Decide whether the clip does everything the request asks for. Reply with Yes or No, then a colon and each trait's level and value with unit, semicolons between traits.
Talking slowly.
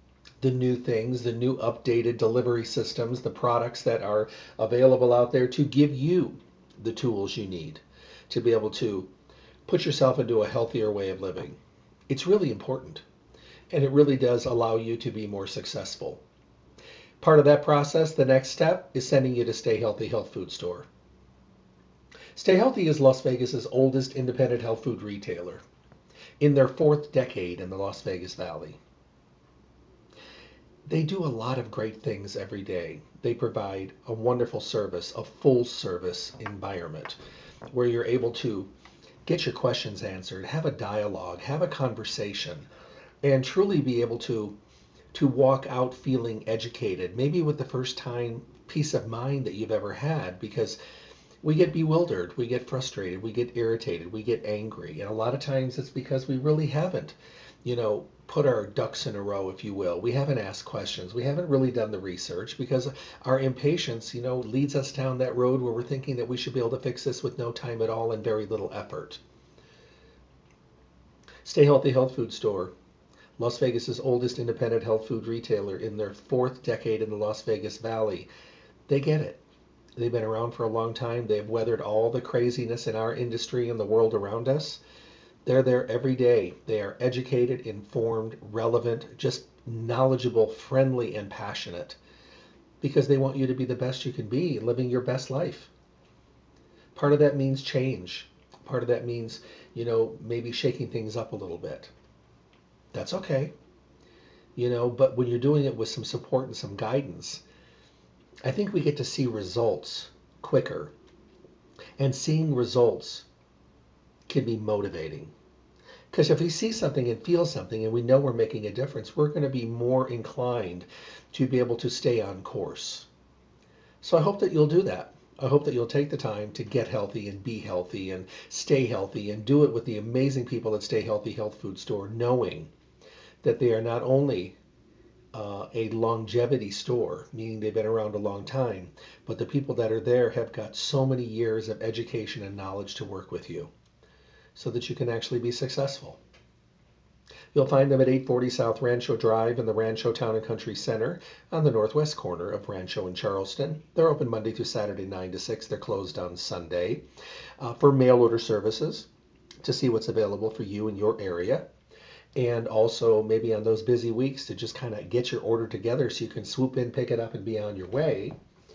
No: average, 185 wpm